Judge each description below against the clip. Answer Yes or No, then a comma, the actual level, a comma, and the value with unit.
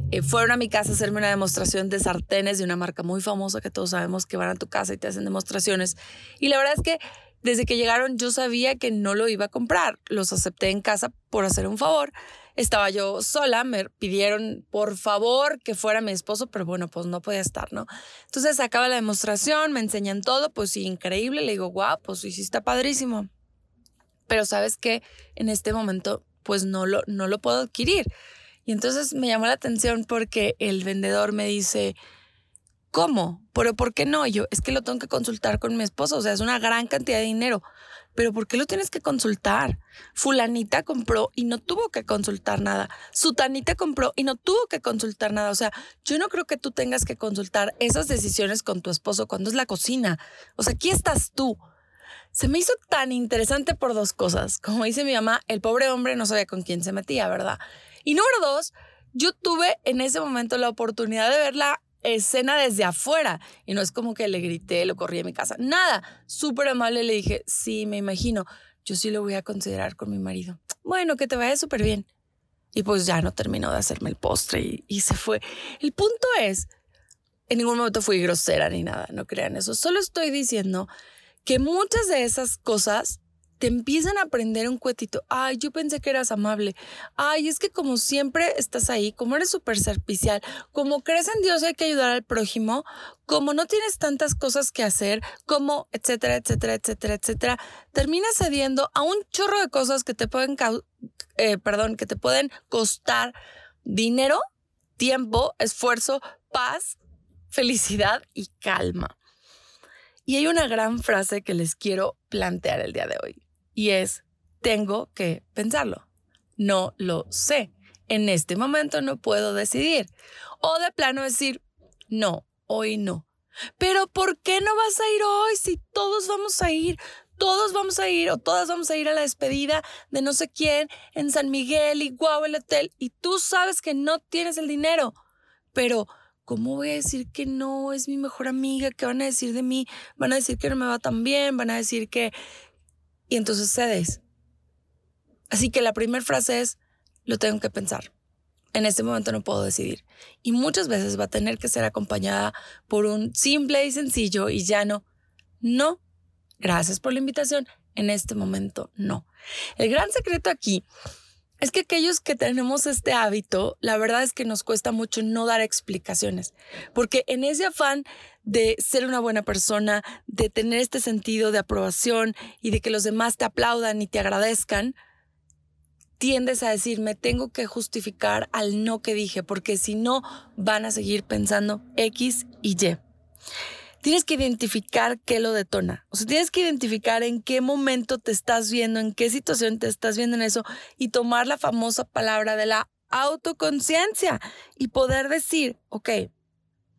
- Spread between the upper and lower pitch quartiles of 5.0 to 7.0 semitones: Yes, wide, 5.5 semitones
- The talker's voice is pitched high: Yes, high, 230 Hz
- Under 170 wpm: No, fast, 190 wpm